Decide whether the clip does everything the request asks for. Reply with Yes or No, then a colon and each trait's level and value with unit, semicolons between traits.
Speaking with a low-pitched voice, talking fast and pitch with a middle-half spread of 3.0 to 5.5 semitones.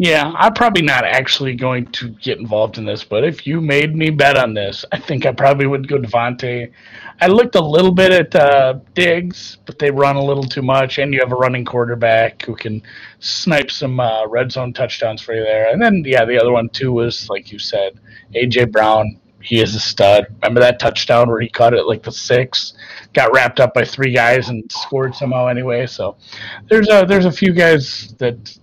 Yes: low, 130 Hz; fast, 220 wpm; average, 3.7 semitones